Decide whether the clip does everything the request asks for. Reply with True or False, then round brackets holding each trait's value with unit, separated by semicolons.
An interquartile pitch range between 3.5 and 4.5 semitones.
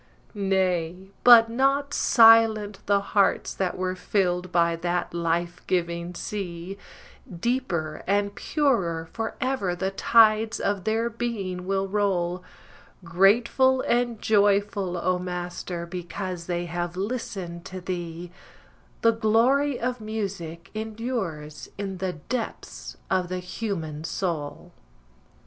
True (4.1 semitones)